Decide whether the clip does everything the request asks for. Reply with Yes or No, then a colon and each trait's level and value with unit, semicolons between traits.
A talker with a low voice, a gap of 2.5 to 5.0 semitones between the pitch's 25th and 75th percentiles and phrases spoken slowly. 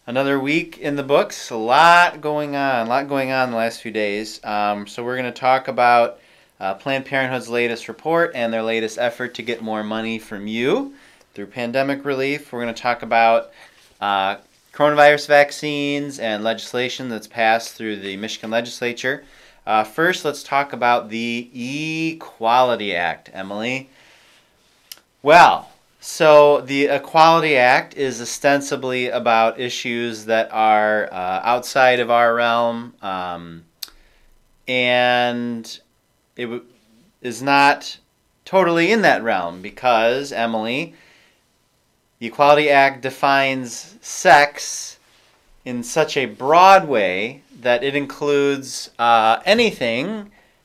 Yes: low, 125 Hz; average, 3.8 semitones; slow, 130 wpm